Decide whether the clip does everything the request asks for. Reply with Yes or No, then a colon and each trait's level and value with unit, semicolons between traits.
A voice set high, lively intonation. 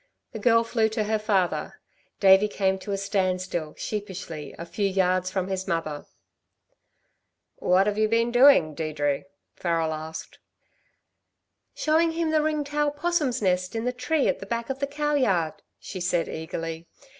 Yes: high, 195 Hz; wide, 6.0 semitones